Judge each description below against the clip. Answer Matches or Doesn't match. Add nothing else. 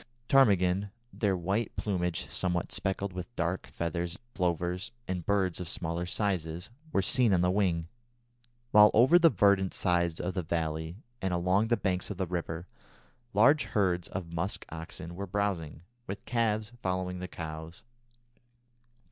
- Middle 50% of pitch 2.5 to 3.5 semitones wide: Matches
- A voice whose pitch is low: Matches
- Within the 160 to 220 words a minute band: Doesn't match